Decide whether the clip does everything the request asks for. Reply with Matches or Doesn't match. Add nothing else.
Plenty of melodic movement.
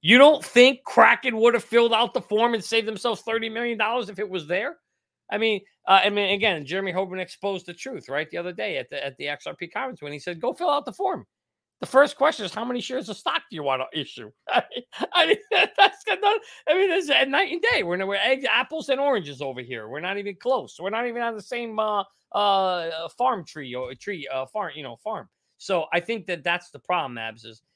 Matches